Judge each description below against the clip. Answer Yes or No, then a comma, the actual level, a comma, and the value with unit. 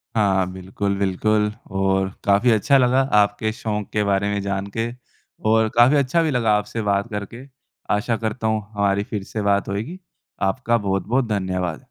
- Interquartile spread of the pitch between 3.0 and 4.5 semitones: No, narrow, 2.5 semitones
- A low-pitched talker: Yes, low, 105 Hz